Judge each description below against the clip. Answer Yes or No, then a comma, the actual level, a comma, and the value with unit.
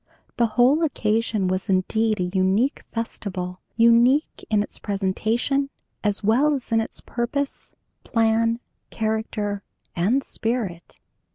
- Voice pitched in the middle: No, high, 225 Hz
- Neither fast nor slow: No, slow, 115 wpm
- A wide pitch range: No, average, 3.1 semitones